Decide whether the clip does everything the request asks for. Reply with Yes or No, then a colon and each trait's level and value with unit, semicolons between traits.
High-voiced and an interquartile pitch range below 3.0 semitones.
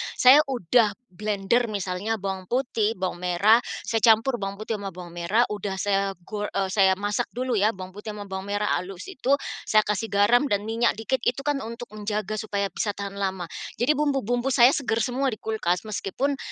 No: high, 210 Hz; average, 3.4 semitones